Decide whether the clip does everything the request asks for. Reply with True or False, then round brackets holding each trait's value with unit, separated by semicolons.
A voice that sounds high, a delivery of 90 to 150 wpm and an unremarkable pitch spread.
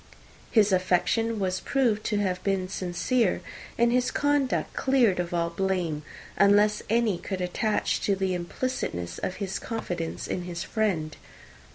True (195 Hz; 145 wpm; 4.0 semitones)